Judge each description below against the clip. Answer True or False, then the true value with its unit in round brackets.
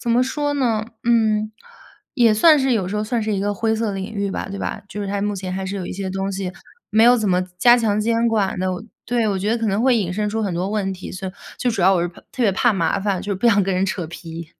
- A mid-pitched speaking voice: False (205 Hz)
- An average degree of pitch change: True (3.1 semitones)